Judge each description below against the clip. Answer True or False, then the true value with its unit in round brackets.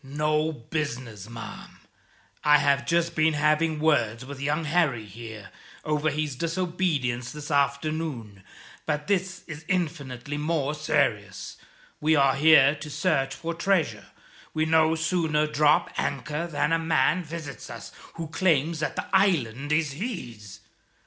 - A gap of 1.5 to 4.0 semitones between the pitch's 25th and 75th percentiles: True (3.0 semitones)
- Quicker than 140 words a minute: False (135 wpm)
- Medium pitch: True (150 Hz)